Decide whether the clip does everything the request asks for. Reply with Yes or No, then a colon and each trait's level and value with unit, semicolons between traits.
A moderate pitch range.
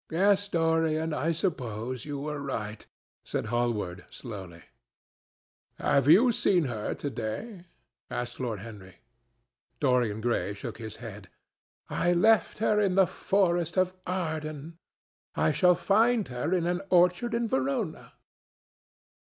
No: wide, 7.6 semitones